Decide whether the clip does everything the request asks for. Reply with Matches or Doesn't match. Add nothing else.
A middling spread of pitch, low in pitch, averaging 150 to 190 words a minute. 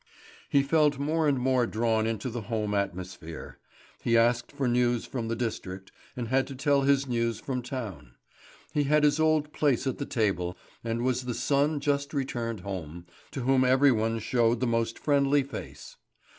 Matches